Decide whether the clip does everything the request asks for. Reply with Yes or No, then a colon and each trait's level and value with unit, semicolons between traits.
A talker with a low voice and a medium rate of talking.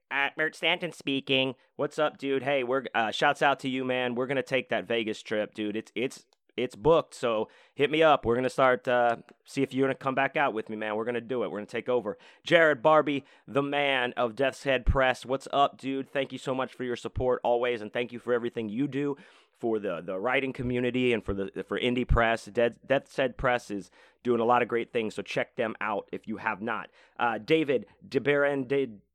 No: low, 130 Hz; fast, 235 wpm